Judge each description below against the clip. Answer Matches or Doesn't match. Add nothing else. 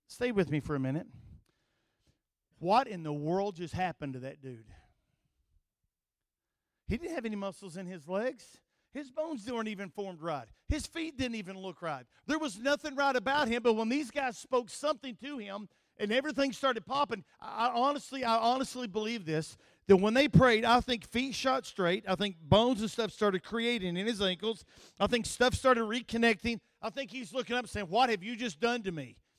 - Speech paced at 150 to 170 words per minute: Doesn't match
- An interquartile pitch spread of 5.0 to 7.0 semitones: Matches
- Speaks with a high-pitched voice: Matches